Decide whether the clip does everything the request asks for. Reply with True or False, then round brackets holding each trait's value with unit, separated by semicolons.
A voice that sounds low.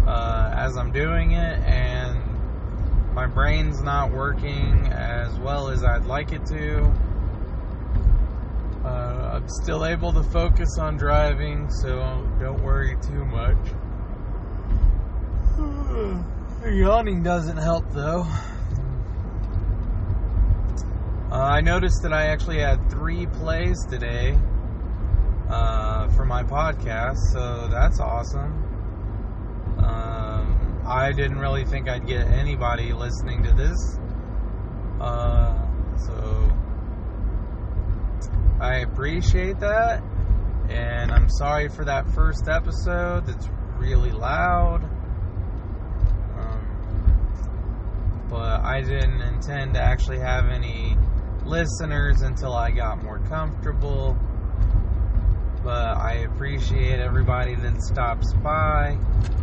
True (95 Hz)